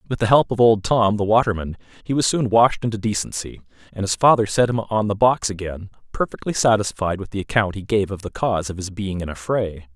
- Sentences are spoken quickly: Yes, fast, 235 wpm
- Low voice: Yes, low, 105 Hz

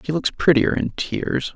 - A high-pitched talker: No, medium, 145 Hz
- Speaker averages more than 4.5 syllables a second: No, 4.3 syllables/s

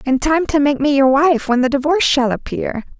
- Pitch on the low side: No, very high, 280 Hz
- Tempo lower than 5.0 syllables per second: No, 5.4 syllables/s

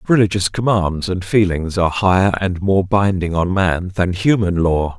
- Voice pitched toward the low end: Yes, very low, 95 Hz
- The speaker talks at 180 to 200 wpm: No, average, 170 wpm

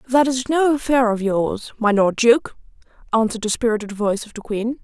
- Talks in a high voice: Yes, high, 230 Hz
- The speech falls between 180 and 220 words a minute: Yes, average, 200 wpm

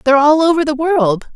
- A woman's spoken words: Yes, female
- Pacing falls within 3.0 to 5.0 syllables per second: No, 5.9 syllables/s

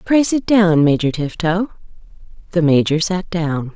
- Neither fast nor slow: Yes, average, 145 wpm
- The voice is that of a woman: Yes, female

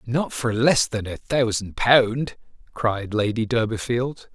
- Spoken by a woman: No, male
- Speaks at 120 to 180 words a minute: Yes, average, 140 wpm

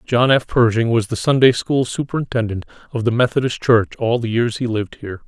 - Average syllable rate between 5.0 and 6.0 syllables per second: Yes, 5.9 syllables/s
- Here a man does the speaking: Yes, male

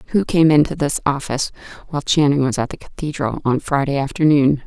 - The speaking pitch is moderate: Yes, medium, 145 Hz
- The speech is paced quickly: No, average, 180 wpm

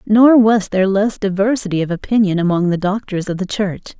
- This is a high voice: Yes, high, 200 Hz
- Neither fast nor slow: Yes, average, 195 wpm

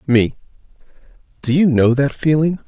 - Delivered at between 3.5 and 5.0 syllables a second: Yes, 4.8 syllables/s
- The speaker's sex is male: Yes, male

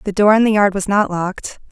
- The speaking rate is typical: No, fast, 280 wpm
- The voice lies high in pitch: Yes, high, 200 Hz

